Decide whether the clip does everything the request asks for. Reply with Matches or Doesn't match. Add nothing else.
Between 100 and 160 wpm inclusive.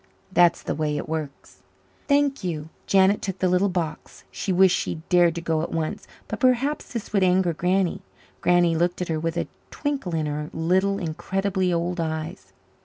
Doesn't match